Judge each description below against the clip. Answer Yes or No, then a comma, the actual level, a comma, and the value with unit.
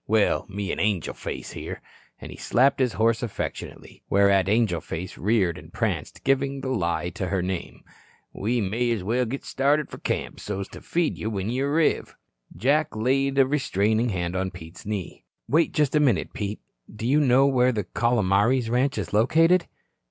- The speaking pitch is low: Yes, low, 115 Hz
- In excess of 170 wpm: Yes, average, 180 wpm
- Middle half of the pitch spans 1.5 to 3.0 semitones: No, wide, 5.4 semitones